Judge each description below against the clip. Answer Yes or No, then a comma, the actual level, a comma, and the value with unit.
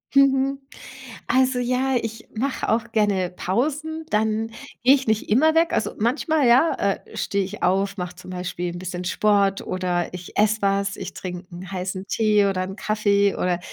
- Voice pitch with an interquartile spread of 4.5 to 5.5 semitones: Yes, average, 5.0 semitones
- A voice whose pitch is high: Yes, high, 210 Hz